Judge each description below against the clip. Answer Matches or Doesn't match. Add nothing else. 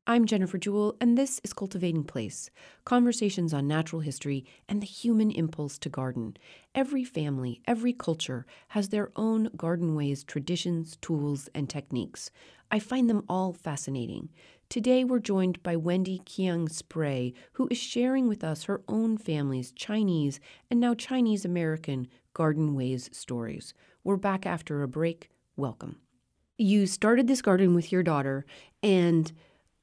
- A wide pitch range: Matches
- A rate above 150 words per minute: Doesn't match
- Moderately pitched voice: Matches